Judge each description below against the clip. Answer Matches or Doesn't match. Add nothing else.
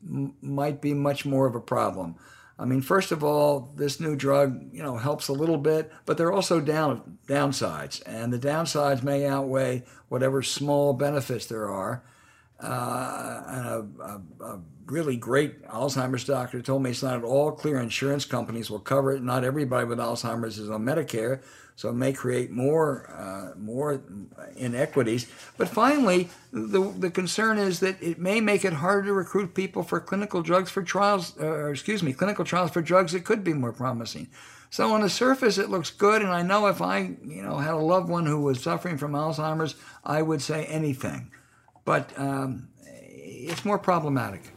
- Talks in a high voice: Doesn't match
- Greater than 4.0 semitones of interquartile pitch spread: Matches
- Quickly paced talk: Doesn't match